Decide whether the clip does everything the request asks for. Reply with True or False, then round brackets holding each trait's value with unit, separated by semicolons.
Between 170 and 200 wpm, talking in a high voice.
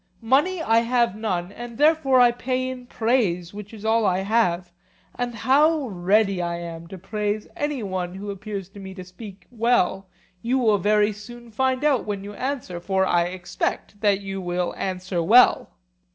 True (180 wpm; 210 Hz)